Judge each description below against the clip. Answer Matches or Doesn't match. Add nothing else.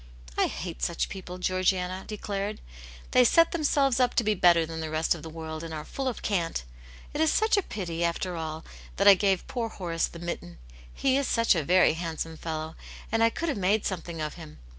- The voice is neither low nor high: Matches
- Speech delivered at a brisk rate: Matches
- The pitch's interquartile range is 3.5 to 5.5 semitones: Matches